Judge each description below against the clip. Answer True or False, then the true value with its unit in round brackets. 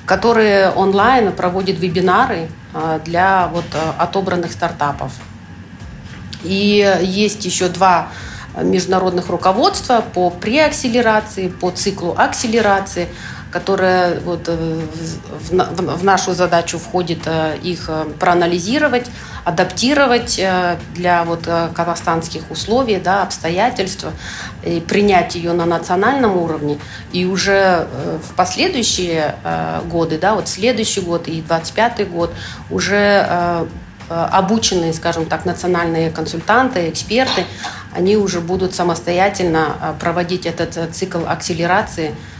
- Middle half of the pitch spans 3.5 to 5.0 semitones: False (2.6 semitones)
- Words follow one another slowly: True (95 wpm)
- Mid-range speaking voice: True (180 Hz)